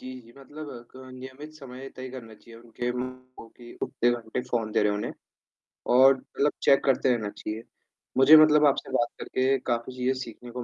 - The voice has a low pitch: Yes, low, 125 Hz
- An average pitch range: No, narrow, 2.2 semitones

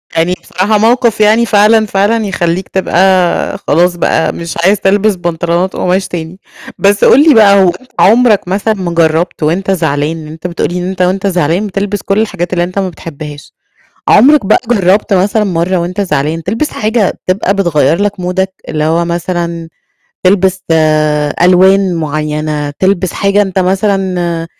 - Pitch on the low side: No, medium, 185 Hz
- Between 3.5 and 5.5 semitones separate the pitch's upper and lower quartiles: No, average, 2.9 semitones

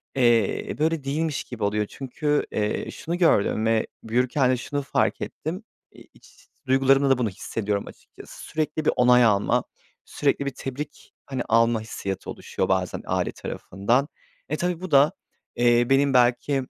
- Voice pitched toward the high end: No, low, 130 Hz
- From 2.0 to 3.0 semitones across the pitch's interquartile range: No, average, 4.0 semitones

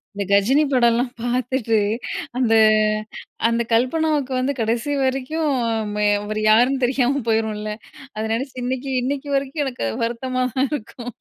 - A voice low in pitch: No, very high, 255 Hz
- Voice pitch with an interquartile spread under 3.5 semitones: Yes, average, 2.9 semitones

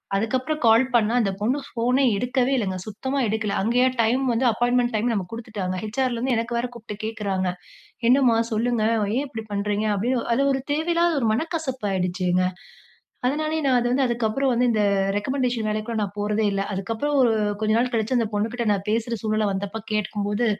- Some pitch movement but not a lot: Yes, average, 3.2 semitones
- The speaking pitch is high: Yes, high, 230 Hz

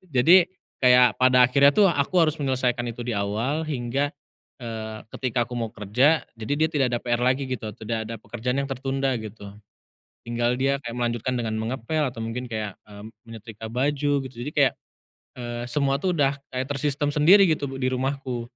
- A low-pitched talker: Yes, low, 125 Hz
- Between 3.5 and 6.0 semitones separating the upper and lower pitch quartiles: No, average, 3.0 semitones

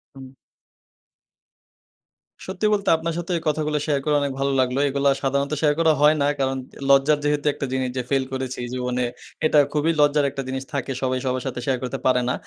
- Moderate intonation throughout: No, narrow, 2.3 semitones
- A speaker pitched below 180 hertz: Yes, medium, 140 Hz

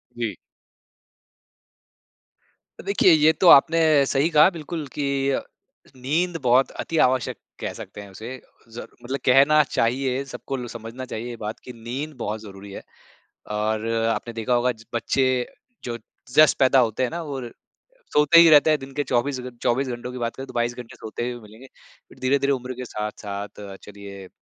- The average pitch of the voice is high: No, low, 125 Hz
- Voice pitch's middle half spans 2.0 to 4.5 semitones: Yes, average, 3.5 semitones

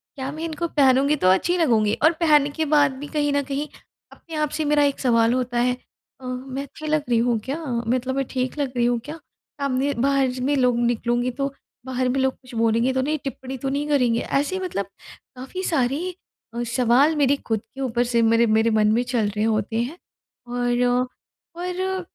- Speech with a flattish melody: No, average, 3.3 semitones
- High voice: Yes, very high, 265 Hz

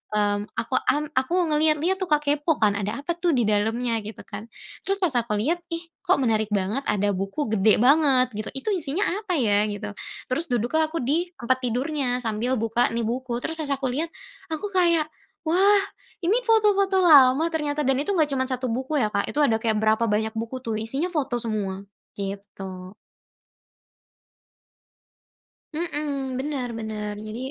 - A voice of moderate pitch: No, very high, 260 Hz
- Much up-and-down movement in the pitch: Yes, wide, 6.2 semitones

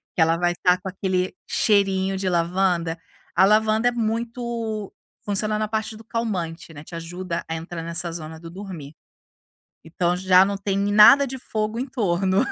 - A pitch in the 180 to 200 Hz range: Yes, high, 190 Hz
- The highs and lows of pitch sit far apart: No, average, 3.9 semitones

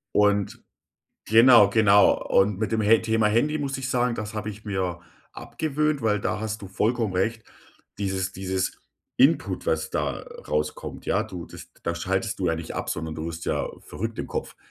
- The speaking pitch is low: Yes, low, 105 Hz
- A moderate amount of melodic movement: Yes, average, 3.2 semitones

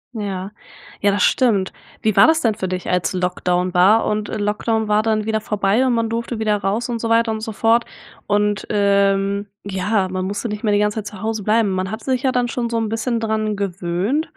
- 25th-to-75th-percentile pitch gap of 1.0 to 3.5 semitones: Yes, narrow, 2.4 semitones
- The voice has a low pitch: No, high, 210 Hz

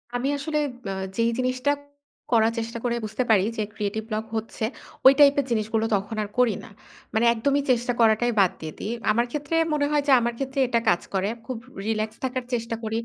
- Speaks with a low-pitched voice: No, high, 230 Hz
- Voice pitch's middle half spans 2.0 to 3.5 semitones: Yes, average, 2.7 semitones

